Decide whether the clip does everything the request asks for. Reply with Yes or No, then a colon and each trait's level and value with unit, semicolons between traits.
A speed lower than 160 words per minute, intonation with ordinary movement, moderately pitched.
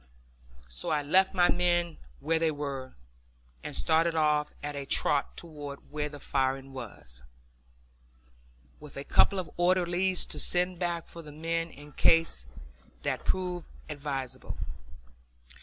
Yes: slow, 135 wpm; average, 3.7 semitones; medium, 155 Hz